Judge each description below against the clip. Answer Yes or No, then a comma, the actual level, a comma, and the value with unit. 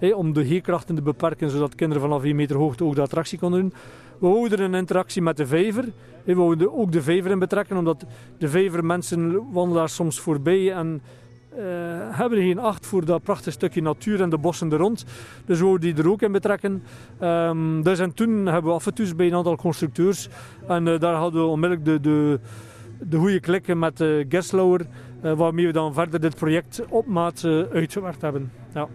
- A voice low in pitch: No, medium, 170 Hz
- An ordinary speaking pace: No, fast, 210 wpm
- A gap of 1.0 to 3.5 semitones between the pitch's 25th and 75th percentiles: Yes, average, 2.9 semitones